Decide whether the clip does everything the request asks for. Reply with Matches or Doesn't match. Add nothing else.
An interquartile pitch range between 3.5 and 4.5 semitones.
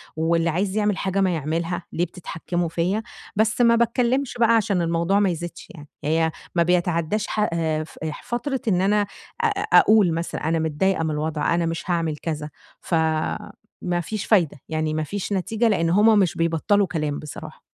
Matches